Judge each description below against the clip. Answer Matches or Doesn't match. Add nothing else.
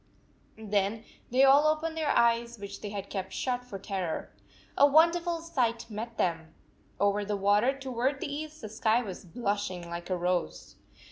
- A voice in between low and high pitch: Doesn't match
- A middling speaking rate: Matches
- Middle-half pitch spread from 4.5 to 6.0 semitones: Matches